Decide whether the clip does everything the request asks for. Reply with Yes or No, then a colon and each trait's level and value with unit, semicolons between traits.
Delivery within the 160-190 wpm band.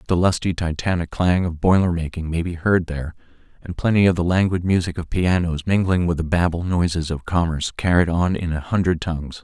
No: fast, 205 wpm